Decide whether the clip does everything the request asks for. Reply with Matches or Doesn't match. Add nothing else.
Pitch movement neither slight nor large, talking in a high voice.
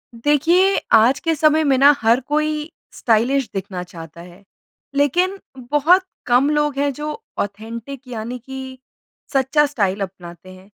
Doesn't match